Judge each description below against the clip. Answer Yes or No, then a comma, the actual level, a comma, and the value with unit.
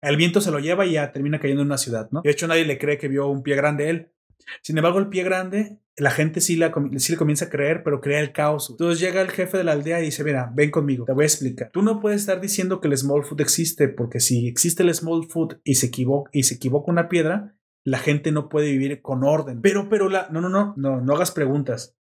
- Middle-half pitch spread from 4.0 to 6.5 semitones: No, average, 3.4 semitones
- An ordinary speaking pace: No, fast, 270 wpm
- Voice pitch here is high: No, medium, 150 Hz